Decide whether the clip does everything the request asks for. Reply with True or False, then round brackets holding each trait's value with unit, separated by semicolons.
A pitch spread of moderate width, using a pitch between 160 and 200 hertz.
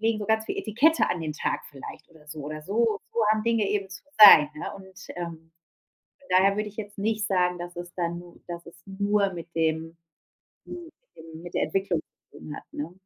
True (4.1 semitones; 185 Hz)